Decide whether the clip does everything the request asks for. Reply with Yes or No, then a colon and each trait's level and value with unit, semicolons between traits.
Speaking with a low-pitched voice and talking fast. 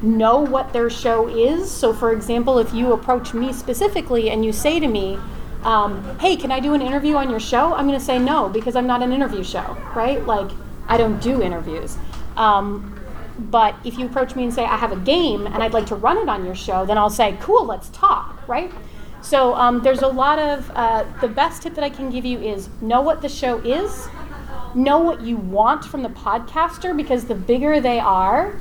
No: high, 245 Hz; fast, 220 wpm